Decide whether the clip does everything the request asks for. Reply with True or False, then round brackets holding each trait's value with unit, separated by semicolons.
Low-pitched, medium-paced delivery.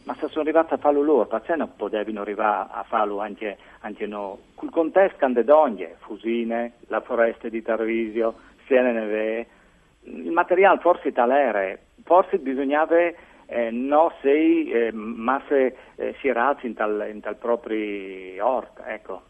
True (120 Hz; 145 wpm)